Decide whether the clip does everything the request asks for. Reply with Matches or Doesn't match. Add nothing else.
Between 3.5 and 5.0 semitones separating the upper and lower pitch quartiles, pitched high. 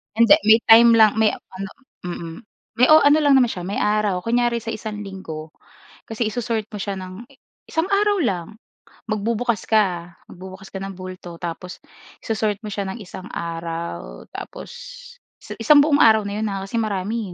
Matches